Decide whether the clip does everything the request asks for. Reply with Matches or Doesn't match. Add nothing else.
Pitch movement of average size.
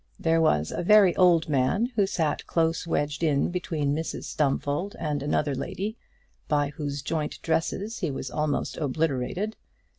Matches